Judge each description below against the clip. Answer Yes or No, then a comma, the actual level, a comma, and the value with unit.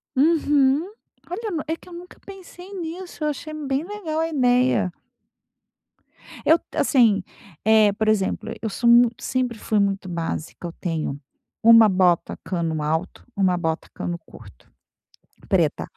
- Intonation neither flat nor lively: No, wide, 8.9 semitones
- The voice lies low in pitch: No, high, 235 Hz